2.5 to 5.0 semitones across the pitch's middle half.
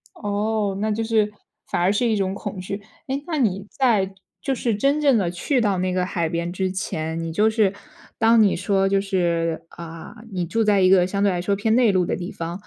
Yes: average, 3.4 semitones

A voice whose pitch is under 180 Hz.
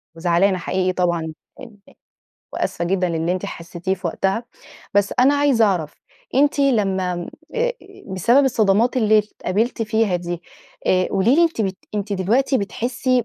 No: high, 200 Hz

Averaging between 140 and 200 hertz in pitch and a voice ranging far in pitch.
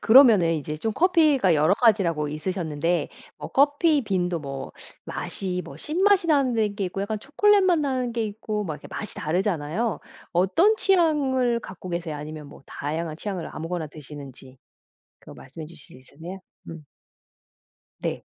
Yes: high, 190 Hz; wide, 8.6 semitones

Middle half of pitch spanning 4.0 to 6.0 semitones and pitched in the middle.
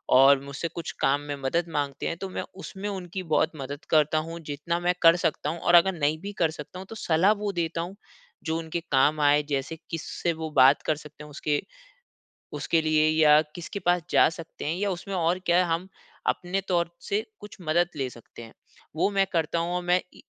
No: average, 2.9 semitones; medium, 165 Hz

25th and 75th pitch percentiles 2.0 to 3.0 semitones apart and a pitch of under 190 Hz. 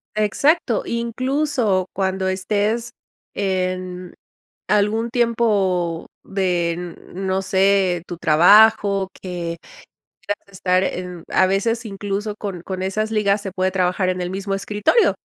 No: narrow, 2.6 semitones; high, 195 Hz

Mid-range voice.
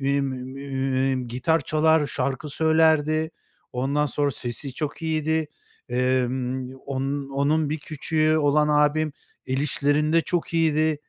Yes: medium, 145 Hz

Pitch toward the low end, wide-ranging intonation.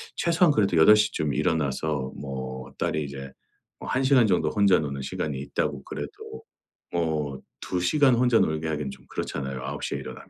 Yes: very low, 75 Hz; wide, 7.0 semitones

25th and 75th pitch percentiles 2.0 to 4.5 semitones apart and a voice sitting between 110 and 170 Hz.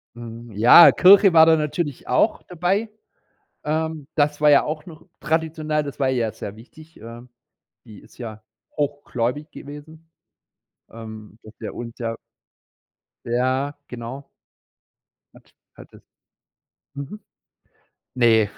No: average, 5.1 semitones; medium, 140 Hz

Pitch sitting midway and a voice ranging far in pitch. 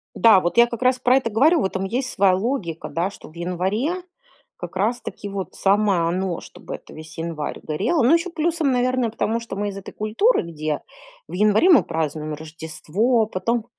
No: high, 210 Hz; wide, 6.2 semitones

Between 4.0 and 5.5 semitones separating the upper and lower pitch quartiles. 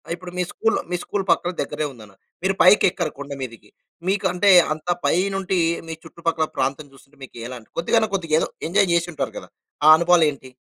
Yes: average, 4.7 semitones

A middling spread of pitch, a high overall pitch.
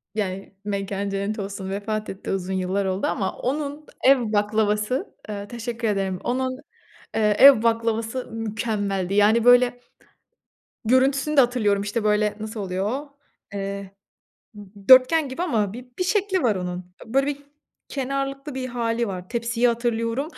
Yes: average, 4.3 semitones; high, 225 Hz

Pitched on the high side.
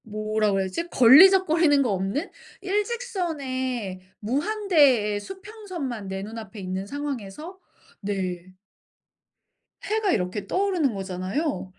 Yes: very high, 255 Hz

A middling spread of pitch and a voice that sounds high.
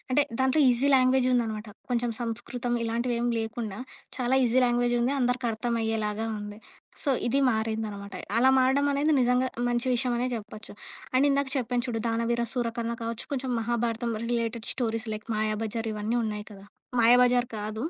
No: narrow, 1.9 semitones; high, 235 Hz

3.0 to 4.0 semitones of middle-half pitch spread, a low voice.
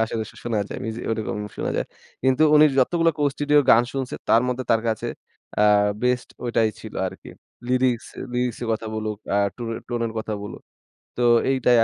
No: narrow, 2.5 semitones; low, 120 Hz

